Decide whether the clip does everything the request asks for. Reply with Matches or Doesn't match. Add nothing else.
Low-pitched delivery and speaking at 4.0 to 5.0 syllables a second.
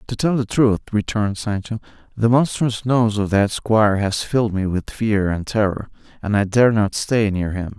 Matches